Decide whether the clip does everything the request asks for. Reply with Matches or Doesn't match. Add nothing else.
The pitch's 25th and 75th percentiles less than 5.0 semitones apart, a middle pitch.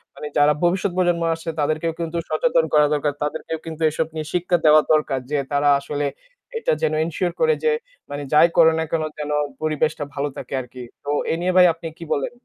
Matches